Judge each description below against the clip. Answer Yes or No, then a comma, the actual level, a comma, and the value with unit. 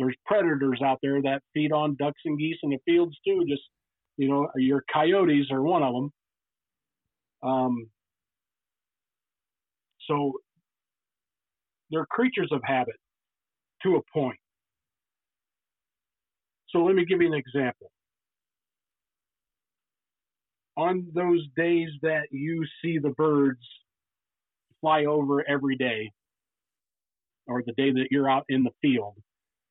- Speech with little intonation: No, average, 3.7 semitones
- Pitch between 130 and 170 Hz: Yes, medium, 140 Hz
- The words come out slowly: Yes, slow, 120 wpm